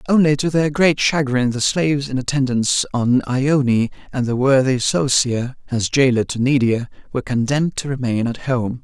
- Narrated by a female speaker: No, male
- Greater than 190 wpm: No, average, 170 wpm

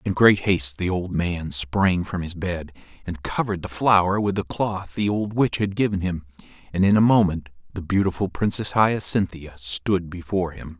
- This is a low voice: Yes, very low, 90 Hz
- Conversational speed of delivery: Yes, average, 190 wpm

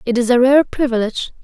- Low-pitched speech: No, very high, 250 Hz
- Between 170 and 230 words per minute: Yes, fast, 210 wpm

